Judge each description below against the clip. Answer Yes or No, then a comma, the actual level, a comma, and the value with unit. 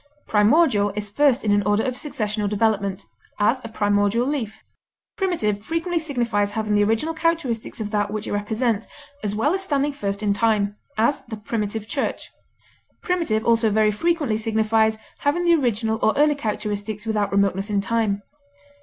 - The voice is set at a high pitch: Yes, high, 220 Hz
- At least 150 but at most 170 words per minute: Yes, average, 165 wpm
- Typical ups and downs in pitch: Yes, average, 4.4 semitones